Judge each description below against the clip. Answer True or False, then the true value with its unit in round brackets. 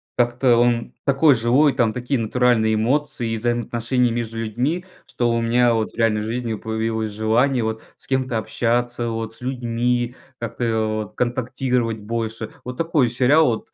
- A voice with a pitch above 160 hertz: False (120 Hz)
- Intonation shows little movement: True (1.8 semitones)